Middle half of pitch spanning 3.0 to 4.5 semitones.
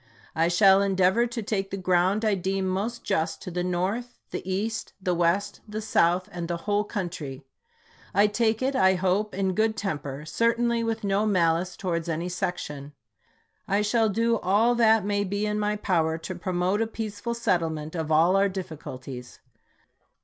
Yes: average, 3.5 semitones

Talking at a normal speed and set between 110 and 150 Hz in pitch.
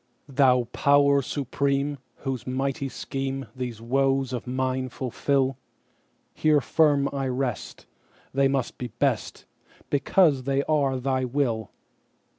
No: slow, 100 wpm; low, 135 Hz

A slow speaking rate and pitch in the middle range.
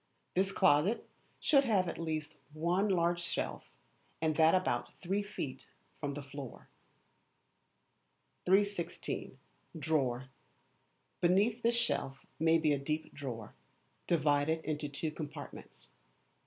Yes: slow, 115 wpm; medium, 160 Hz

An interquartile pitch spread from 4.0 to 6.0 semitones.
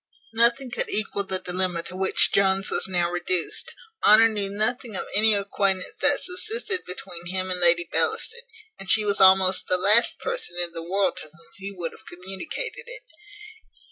No: average, 3.6 semitones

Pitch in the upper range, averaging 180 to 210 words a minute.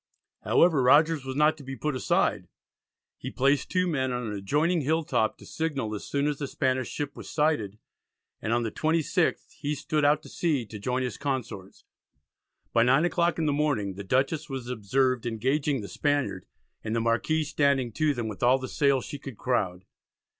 No: low, 135 Hz; average, 190 wpm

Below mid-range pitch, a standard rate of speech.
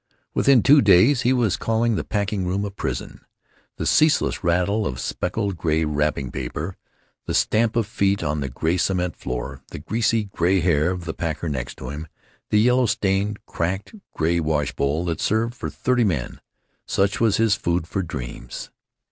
Yes: very low, 95 Hz; average, 175 wpm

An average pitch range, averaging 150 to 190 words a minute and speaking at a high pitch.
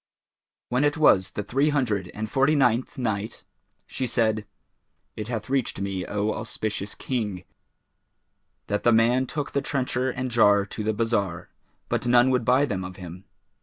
No: average, 4.0 semitones; average, 165 wpm; low, 115 Hz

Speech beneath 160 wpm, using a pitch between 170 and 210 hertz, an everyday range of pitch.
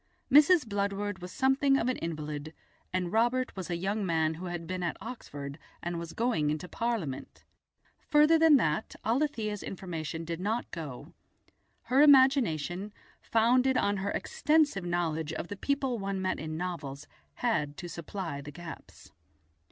No: average, 150 wpm; high, 190 Hz; wide, 6.8 semitones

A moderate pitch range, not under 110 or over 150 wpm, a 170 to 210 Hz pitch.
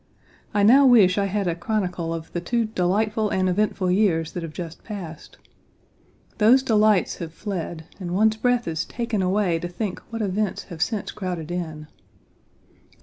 No: average, 3.8 semitones; average, 165 wpm; high, 190 Hz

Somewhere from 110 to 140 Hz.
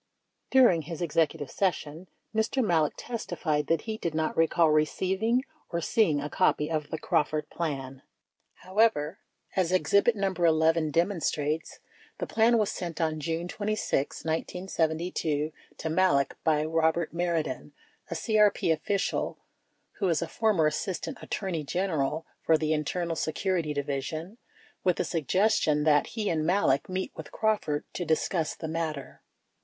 No: medium, 165 Hz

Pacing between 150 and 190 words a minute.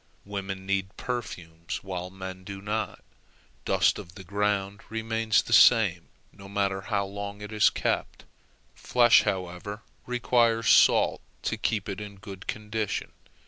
No: average, 140 wpm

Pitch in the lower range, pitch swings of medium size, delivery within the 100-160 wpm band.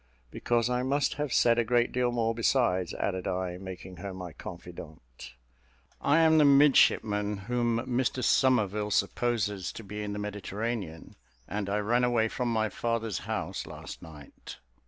Yes: low, 110 Hz; average, 4.4 semitones; average, 155 wpm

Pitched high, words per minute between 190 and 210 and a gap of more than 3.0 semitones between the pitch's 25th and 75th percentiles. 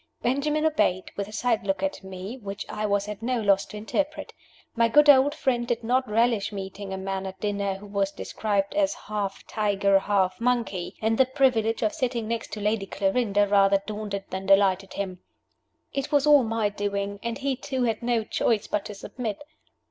Yes: high, 210 Hz; average, 195 wpm; average, 3.6 semitones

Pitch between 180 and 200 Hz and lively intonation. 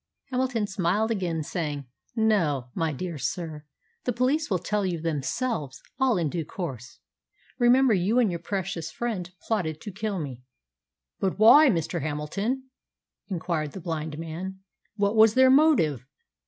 Yes: medium, 185 Hz; wide, 5.9 semitones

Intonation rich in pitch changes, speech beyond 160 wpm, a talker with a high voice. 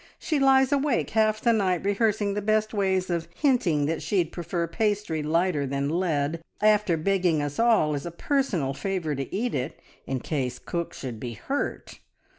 No: wide, 6.0 semitones; average, 175 wpm; medium, 180 Hz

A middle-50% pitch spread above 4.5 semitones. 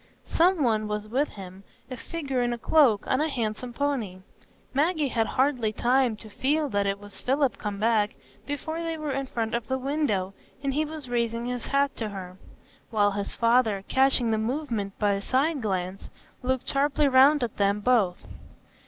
Yes: average, 4.9 semitones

